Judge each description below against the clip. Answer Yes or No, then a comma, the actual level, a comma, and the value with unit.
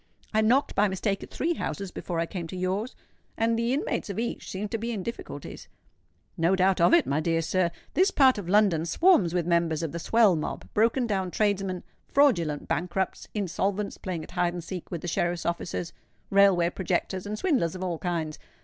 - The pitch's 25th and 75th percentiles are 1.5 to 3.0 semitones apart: No, average, 3.9 semitones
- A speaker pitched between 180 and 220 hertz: Yes, high, 190 Hz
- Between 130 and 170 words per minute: No, average, 200 wpm